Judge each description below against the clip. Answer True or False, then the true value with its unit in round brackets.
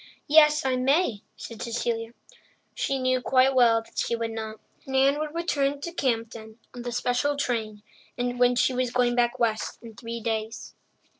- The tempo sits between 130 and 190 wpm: True (165 wpm)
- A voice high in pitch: True (245 Hz)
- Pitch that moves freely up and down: False (2.7 semitones)